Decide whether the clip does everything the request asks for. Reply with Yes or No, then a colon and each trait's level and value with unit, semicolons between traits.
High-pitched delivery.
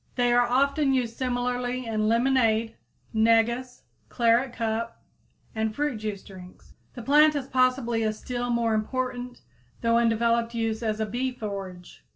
Yes: high, 235 Hz